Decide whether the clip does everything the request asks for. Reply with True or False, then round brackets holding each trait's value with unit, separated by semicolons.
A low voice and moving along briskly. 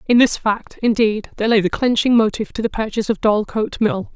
False (220 Hz; 215 wpm)